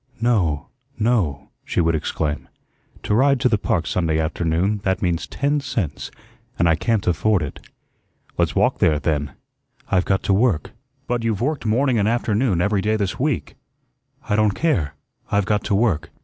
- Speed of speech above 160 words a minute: Yes, average, 170 wpm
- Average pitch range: No, wide, 5.8 semitones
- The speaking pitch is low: Yes, low, 100 Hz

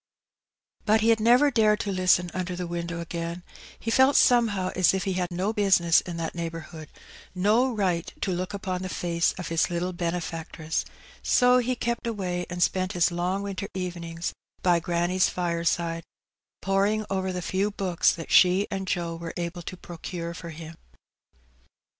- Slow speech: No, average, 170 wpm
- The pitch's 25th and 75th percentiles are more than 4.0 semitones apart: No, average, 2.7 semitones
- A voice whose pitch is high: No, medium, 180 Hz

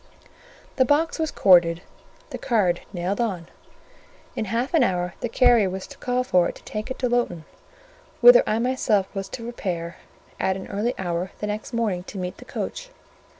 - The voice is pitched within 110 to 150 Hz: No, high, 210 Hz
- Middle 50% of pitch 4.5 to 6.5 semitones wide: Yes, average, 5.1 semitones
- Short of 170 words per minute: No, average, 185 wpm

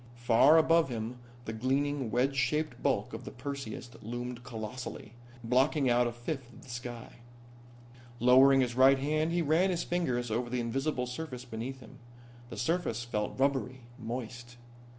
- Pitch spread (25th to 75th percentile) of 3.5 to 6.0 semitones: No, average, 2.7 semitones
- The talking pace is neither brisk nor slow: Yes, average, 155 wpm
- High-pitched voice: No, low, 125 Hz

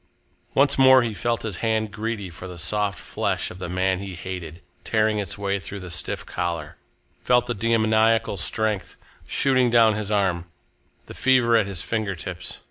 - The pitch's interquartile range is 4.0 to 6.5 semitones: No, average, 3.5 semitones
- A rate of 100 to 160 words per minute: No, average, 175 wpm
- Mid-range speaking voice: No, low, 105 Hz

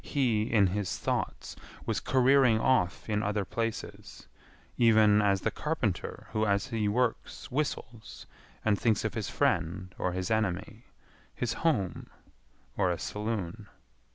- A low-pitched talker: Yes, low, 105 Hz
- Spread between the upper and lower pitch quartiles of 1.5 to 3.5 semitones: Yes, average, 2.8 semitones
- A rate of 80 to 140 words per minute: Yes, slow, 135 wpm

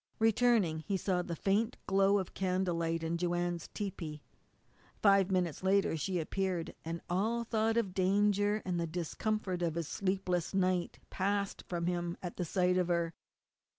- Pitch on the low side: No, medium, 185 Hz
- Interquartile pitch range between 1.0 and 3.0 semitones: Yes, narrow, 2.6 semitones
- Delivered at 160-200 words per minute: No, average, 150 wpm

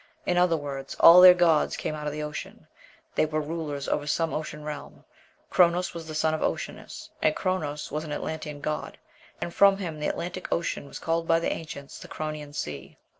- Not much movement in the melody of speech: Yes, narrow, 2.1 semitones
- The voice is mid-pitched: Yes, medium, 155 Hz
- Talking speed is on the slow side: No, average, 200 wpm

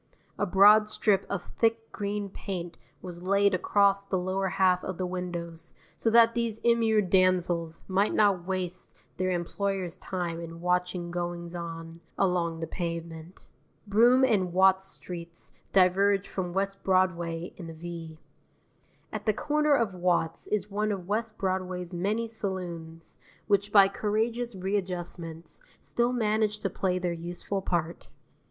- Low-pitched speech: No, medium, 185 Hz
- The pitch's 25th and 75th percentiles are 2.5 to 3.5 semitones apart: Yes, average, 2.8 semitones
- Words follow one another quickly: No, average, 145 wpm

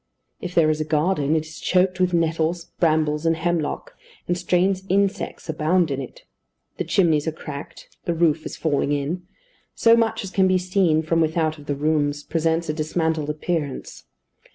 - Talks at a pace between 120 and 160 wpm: No, average, 175 wpm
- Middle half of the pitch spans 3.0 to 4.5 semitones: No, narrow, 2.6 semitones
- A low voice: No, medium, 160 Hz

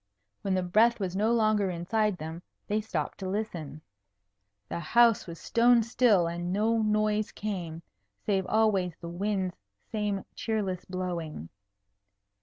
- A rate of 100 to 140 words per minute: Yes, slow, 135 wpm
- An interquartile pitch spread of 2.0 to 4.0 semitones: Yes, average, 3.6 semitones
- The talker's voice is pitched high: Yes, high, 195 Hz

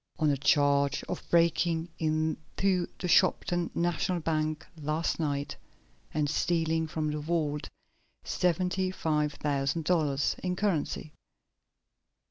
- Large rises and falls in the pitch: No, narrow, 2.5 semitones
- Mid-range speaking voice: Yes, medium, 160 Hz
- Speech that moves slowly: Yes, slow, 110 wpm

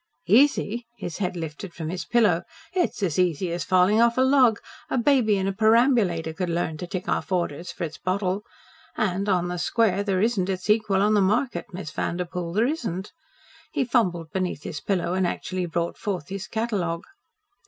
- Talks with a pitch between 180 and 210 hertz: Yes, high, 190 Hz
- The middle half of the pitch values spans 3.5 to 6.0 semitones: Yes, average, 3.9 semitones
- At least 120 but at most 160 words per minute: No, average, 185 wpm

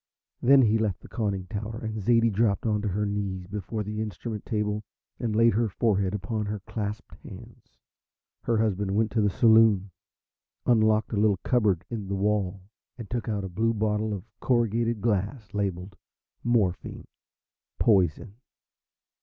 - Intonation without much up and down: Yes, narrow, 2.1 semitones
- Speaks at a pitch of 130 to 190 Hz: No, low, 105 Hz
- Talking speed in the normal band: Yes, average, 155 wpm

